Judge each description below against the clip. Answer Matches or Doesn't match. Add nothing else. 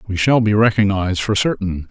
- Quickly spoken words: Doesn't match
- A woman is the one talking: Doesn't match